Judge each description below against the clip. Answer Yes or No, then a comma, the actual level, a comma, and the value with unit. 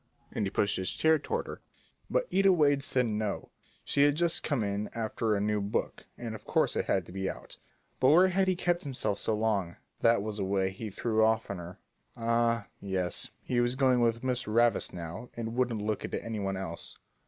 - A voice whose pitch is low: Yes, low, 110 Hz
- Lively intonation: No, average, 4.2 semitones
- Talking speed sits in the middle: No, fast, 215 wpm